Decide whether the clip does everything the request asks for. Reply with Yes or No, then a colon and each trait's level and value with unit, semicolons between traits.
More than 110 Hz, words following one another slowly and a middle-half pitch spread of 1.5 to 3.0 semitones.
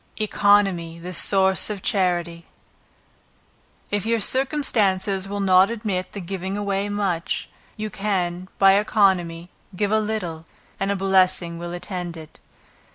Yes: high, 190 Hz; slow, 130 wpm; narrow, 2.6 semitones